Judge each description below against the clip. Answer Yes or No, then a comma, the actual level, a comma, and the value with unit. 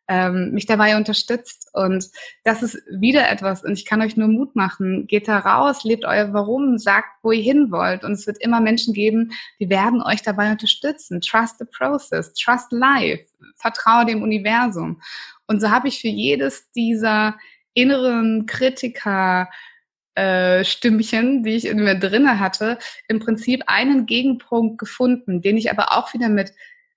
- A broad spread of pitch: No, average, 2.9 semitones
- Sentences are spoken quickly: No, average, 160 wpm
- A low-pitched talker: No, high, 225 Hz